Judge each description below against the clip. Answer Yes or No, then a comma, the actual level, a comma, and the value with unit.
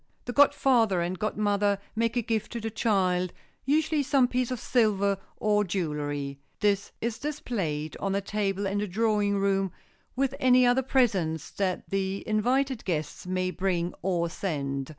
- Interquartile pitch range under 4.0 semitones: No, average, 4.5 semitones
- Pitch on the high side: Yes, high, 200 Hz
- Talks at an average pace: Yes, average, 150 wpm